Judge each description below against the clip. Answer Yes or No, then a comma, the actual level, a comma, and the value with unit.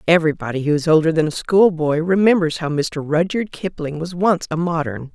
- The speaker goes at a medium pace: Yes, average, 185 wpm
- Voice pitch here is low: No, medium, 165 Hz